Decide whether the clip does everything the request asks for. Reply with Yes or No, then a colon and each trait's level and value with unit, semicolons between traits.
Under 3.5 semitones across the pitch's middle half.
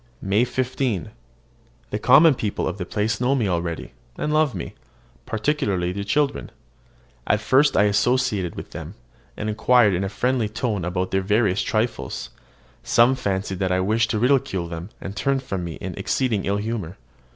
No: average, 4.9 semitones